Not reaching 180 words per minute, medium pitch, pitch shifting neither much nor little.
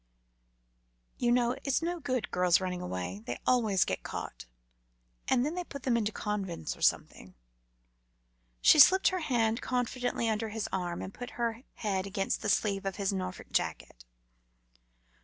No: average, 160 wpm; high, 220 Hz; average, 4.8 semitones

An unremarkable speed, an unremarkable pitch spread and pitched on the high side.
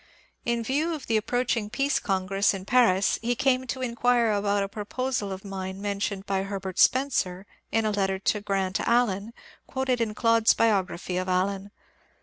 Yes: average, 170 wpm; average, 3.8 semitones; high, 210 Hz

